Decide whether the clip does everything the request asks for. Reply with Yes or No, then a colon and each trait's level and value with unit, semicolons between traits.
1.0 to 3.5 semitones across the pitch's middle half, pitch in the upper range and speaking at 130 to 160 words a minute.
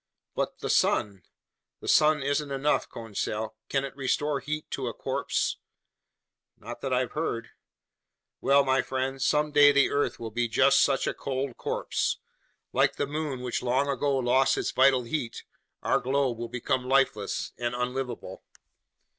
No: narrow, 2.4 semitones; low, 135 Hz; average, 155 wpm